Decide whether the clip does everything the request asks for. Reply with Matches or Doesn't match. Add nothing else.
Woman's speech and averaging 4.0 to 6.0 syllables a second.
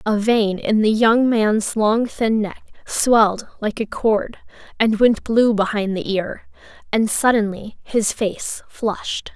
Doesn't match